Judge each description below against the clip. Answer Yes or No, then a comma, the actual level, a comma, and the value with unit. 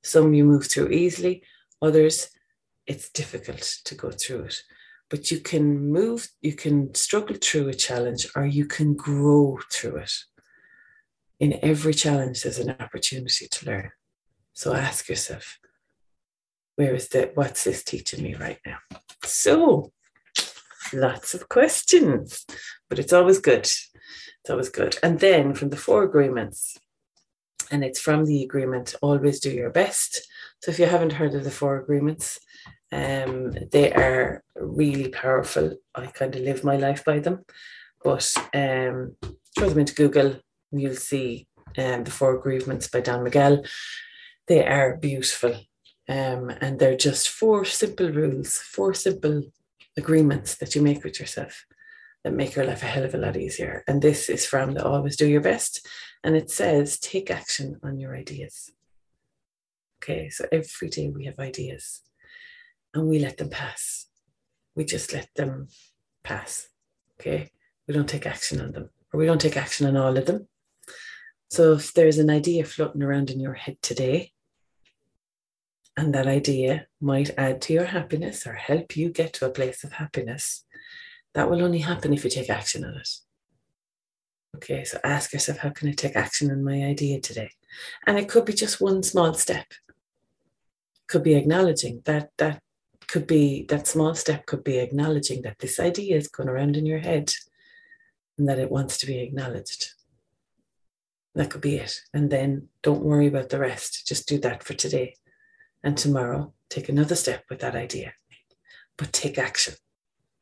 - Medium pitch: Yes, medium, 145 Hz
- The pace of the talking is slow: No, average, 165 wpm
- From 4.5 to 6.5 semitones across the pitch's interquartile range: No, average, 3.6 semitones